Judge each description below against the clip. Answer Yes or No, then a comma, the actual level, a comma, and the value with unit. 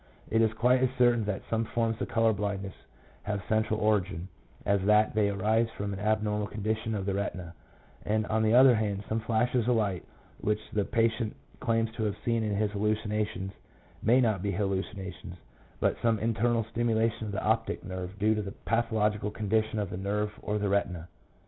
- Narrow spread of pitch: Yes, narrow, 1.9 semitones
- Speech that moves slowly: No, average, 185 wpm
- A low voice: Yes, low, 105 Hz